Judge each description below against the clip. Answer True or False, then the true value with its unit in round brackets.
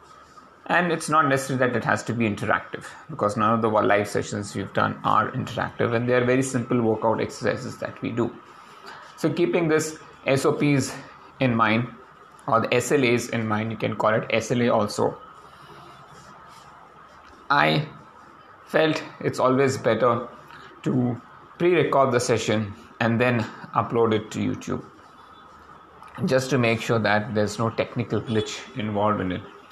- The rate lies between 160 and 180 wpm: False (150 wpm)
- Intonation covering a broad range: False (3.7 semitones)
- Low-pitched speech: True (120 Hz)